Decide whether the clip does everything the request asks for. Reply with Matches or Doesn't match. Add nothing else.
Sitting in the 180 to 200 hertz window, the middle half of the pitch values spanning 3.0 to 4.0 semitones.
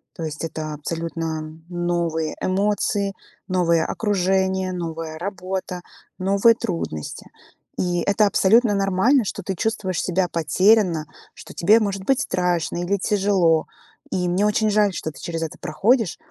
Matches